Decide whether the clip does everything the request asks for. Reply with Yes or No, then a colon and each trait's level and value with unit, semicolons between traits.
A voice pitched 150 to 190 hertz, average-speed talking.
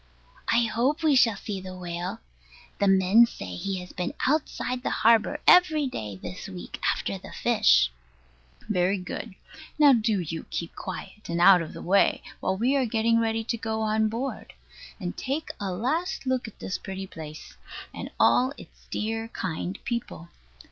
No: high, 215 Hz; average, 170 wpm